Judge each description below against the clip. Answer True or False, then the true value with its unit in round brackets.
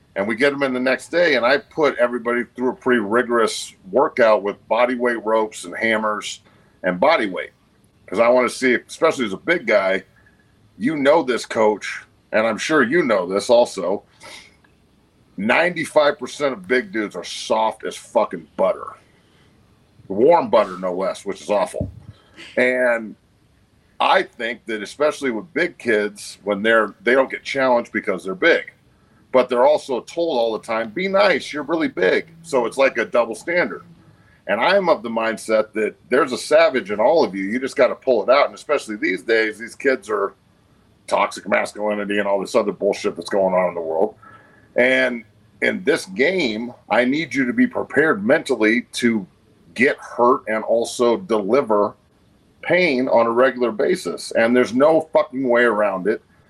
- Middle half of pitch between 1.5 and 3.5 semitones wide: True (3.0 semitones)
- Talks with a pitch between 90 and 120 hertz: True (115 Hz)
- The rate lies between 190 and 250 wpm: False (175 wpm)